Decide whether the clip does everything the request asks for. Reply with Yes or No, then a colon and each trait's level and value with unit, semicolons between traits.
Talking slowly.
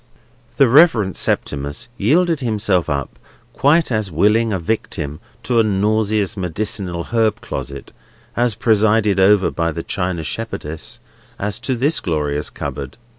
Yes: slow, 130 wpm